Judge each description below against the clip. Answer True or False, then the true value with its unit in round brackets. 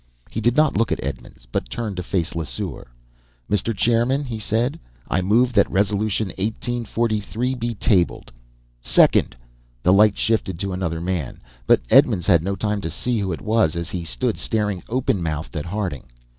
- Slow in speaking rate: False (170 wpm)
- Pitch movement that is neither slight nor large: True (4.3 semitones)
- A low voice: True (100 Hz)